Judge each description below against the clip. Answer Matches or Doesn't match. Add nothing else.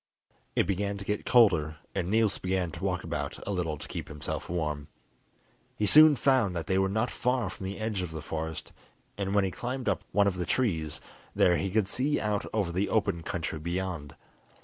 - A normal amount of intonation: Matches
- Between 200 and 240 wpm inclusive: Matches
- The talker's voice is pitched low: Matches